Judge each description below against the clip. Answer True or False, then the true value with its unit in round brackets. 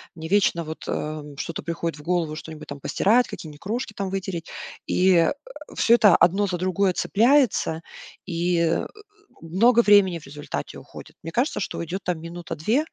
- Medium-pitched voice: True (175 Hz)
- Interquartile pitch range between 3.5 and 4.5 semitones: True (3.9 semitones)